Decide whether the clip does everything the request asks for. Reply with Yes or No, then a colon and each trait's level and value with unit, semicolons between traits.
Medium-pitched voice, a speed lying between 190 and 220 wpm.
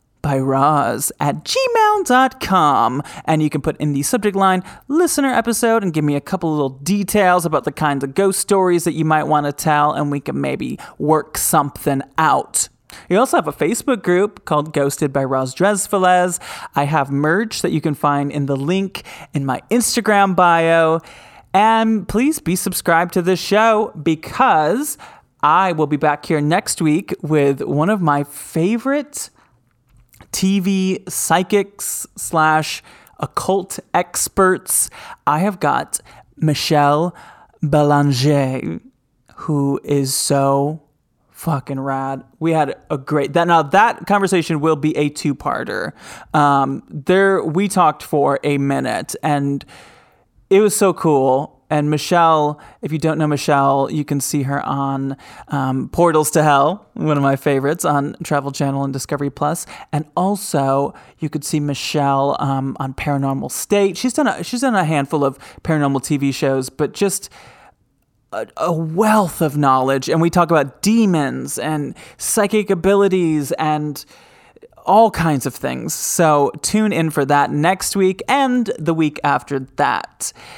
No: medium, 155 Hz; average, 150 wpm